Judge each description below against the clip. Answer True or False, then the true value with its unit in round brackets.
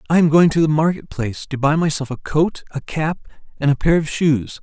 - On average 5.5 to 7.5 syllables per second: True (5.6 syllables/s)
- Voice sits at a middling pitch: True (150 Hz)